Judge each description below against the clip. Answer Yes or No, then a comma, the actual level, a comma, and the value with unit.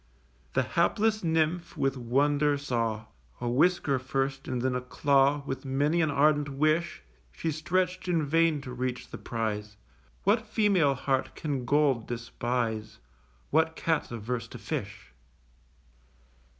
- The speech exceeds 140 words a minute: No, slow, 135 wpm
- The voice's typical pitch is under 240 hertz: Yes, medium, 140 Hz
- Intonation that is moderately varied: Yes, average, 4.4 semitones